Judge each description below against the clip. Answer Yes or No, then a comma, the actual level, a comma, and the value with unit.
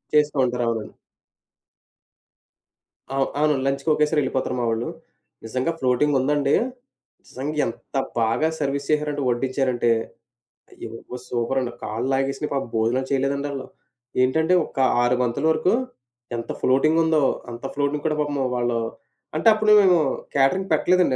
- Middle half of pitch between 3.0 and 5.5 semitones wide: Yes, average, 3.4 semitones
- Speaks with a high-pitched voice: No, low, 135 Hz